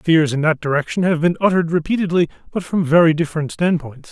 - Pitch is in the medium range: Yes, medium, 165 Hz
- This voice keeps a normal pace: Yes, average, 190 wpm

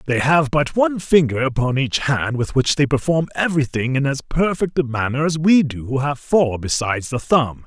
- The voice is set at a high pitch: No, medium, 140 Hz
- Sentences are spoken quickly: Yes, fast, 210 wpm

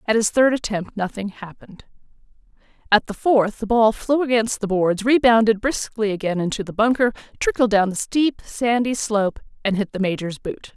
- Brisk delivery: No, average, 180 wpm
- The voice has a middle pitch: No, high, 220 Hz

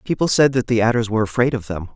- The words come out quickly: Yes, fast, 275 wpm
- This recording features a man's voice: Yes, male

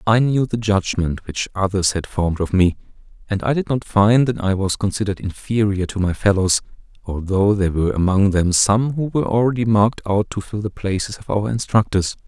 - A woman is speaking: No, male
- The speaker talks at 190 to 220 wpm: Yes, average, 200 wpm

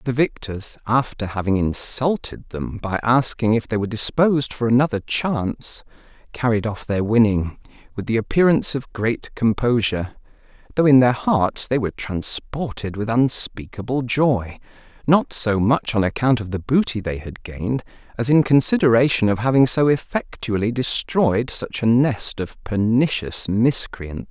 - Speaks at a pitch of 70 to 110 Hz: No, low, 120 Hz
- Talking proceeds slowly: No, average, 150 wpm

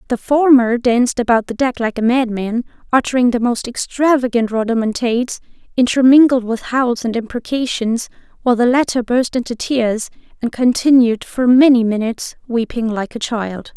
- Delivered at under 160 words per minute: Yes, average, 150 wpm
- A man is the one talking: No, female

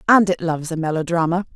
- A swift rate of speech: No, average, 195 wpm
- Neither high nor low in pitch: Yes, medium, 170 Hz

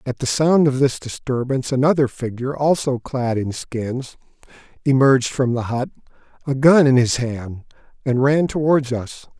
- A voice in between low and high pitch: No, low, 130 Hz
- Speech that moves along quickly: No, average, 160 wpm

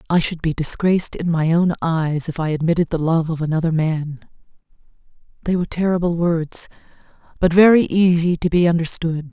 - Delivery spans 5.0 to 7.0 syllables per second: Yes, 5.4 syllables/s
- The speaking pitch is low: No, medium, 165 Hz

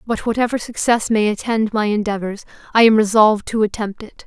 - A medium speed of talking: Yes, average, 185 wpm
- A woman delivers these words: Yes, female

